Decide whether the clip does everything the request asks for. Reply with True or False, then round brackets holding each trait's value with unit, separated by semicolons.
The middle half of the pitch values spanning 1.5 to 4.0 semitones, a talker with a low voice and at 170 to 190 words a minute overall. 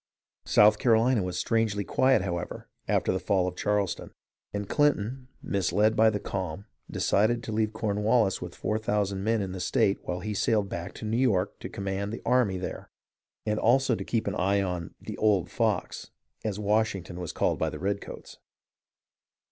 True (2.5 semitones; 105 Hz; 180 wpm)